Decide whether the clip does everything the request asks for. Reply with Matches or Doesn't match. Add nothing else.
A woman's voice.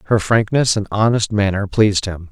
Doesn't match